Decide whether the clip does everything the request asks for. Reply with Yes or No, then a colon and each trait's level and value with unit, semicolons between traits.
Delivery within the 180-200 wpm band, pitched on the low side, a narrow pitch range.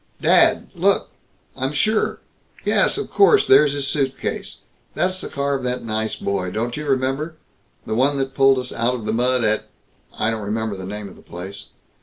No: average, 190 wpm; low, 125 Hz; average, 4.3 semitones